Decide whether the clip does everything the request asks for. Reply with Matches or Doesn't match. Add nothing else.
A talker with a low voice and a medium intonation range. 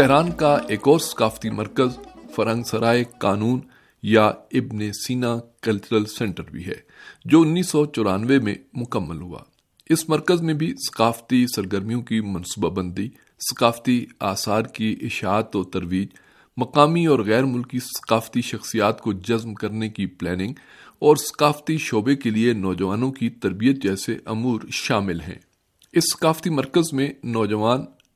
Matches